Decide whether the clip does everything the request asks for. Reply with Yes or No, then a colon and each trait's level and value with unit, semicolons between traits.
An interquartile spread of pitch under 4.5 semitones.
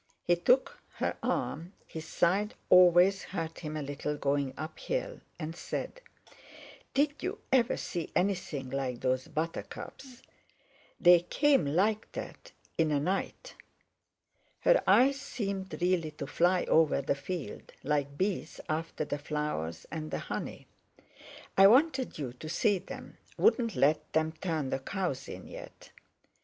No: average, 5.2 semitones